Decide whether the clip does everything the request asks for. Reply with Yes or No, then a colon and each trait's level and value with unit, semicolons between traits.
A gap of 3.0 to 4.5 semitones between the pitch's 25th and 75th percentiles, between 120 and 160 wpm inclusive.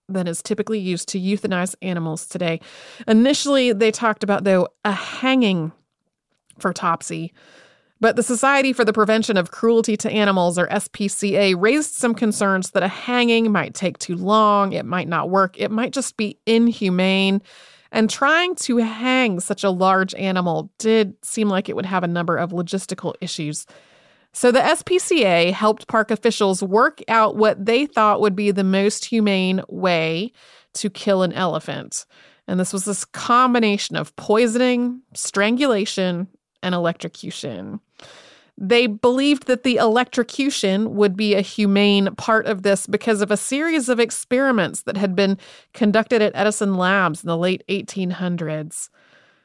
Yes: average, 3.6 semitones; average, 155 wpm